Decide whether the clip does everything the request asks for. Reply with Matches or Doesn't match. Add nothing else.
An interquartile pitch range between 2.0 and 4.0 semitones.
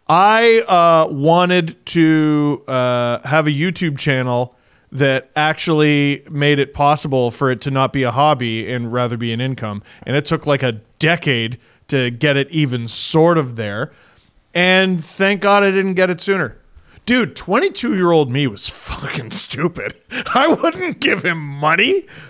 Doesn't match